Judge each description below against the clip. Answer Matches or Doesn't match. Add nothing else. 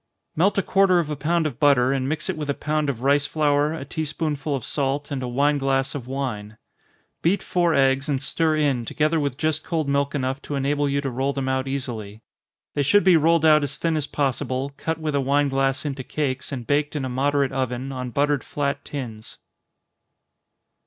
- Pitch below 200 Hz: Matches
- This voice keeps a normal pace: Doesn't match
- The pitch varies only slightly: Matches